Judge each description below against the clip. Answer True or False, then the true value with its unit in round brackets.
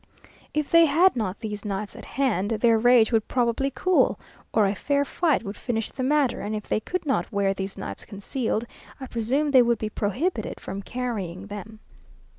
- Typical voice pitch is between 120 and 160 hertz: False (230 Hz)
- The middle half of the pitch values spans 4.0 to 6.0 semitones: True (4.7 semitones)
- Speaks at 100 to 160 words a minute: False (190 wpm)